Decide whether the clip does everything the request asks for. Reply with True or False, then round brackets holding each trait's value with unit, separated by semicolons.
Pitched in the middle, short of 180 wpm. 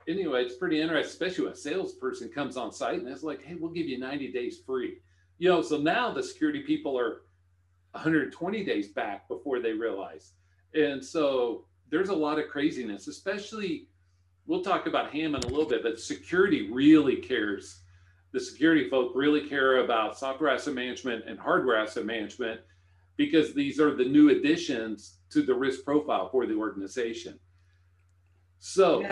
True (145 Hz; 165 wpm)